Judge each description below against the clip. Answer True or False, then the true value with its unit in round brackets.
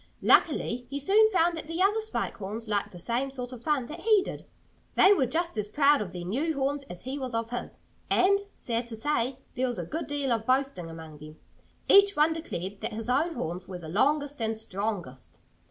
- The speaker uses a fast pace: True (220 wpm)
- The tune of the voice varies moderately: False (6.3 semitones)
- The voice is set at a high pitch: True (255 Hz)